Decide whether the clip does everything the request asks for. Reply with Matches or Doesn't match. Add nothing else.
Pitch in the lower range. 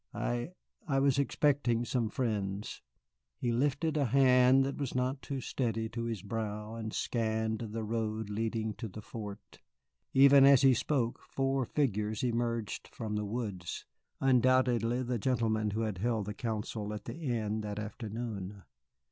Matches